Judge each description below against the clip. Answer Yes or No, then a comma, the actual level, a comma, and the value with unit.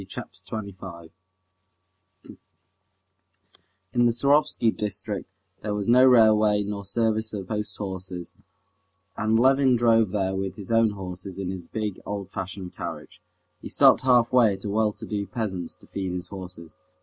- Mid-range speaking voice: No, low, 105 Hz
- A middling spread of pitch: Yes, average, 3.0 semitones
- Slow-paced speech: No, average, 150 wpm